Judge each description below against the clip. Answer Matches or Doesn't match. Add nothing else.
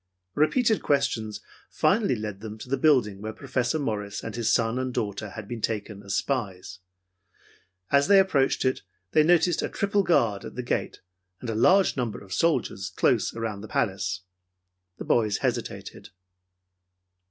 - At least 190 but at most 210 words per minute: Doesn't match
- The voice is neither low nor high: Doesn't match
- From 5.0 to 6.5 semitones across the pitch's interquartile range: Matches